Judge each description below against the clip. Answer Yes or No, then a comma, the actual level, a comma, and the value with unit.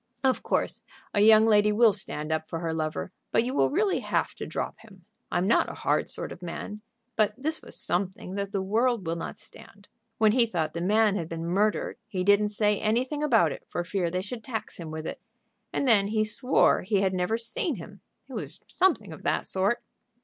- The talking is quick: Yes, fast, 215 wpm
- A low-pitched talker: No, high, 205 Hz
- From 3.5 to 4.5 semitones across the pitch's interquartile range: Yes, average, 3.9 semitones